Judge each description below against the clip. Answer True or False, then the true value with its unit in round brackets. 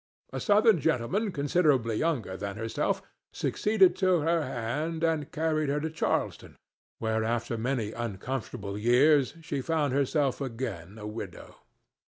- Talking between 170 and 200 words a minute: False (135 wpm)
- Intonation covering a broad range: True (6.0 semitones)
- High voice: False (140 Hz)